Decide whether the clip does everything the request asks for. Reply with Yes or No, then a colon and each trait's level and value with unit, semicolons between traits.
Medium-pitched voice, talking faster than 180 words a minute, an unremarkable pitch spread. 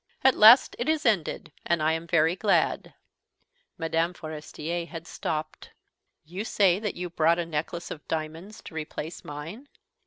No: medium, 170 Hz; average, 155 wpm; average, 3.6 semitones